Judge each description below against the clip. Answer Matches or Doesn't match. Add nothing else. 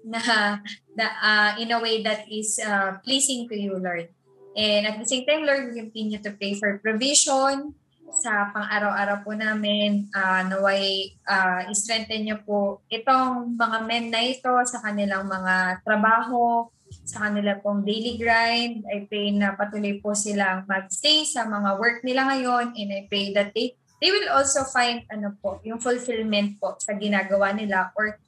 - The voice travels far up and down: Doesn't match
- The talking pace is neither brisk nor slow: Doesn't match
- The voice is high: Matches